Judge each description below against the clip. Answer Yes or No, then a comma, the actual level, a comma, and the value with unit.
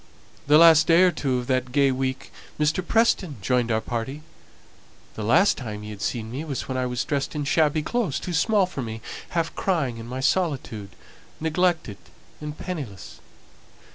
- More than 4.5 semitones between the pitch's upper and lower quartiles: Yes, average, 5.1 semitones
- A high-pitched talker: No, medium, 140 Hz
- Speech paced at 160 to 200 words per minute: Yes, average, 175 wpm